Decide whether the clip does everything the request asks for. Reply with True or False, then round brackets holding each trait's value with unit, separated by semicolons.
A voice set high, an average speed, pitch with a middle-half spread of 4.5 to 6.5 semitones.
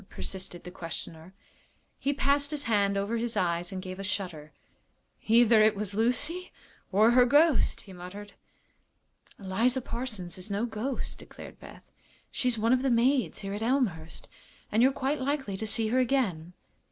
True (220 Hz; 165 wpm; 5.1 semitones)